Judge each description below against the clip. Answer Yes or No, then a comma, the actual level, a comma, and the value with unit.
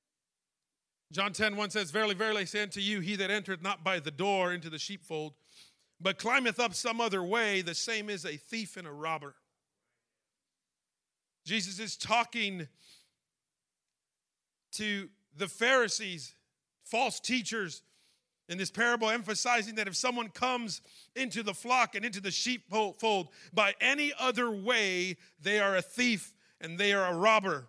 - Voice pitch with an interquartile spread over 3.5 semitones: Yes, average, 4.3 semitones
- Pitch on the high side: Yes, high, 200 Hz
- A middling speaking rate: Yes, average, 150 wpm